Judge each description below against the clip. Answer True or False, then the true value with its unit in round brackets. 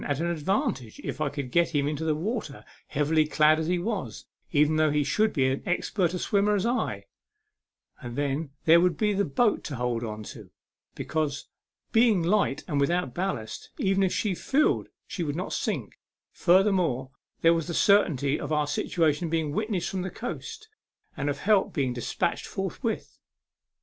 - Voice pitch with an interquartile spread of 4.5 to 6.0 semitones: True (5.0 semitones)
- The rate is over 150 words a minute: True (180 wpm)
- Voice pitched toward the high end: False (160 Hz)